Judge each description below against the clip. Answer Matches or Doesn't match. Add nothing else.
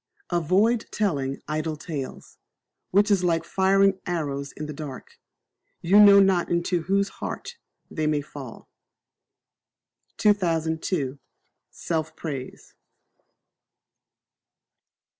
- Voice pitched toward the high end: Doesn't match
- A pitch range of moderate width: Matches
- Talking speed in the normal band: Doesn't match